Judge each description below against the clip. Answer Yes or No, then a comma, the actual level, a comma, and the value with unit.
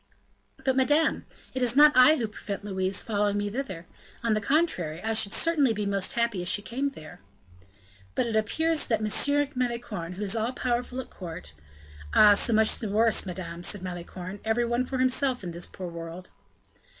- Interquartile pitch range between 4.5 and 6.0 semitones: Yes, average, 5.3 semitones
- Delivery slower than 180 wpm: No, average, 190 wpm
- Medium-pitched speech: No, high, 215 Hz